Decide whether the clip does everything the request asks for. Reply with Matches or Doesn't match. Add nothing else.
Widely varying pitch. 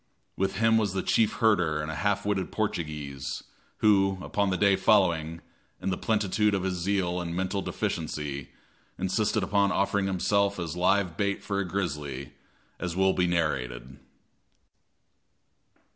Doesn't match